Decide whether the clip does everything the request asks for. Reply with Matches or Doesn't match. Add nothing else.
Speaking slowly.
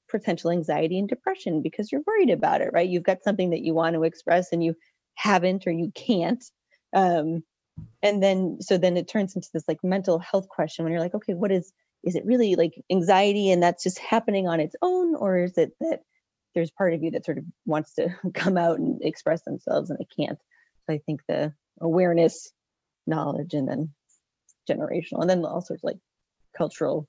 Doesn't match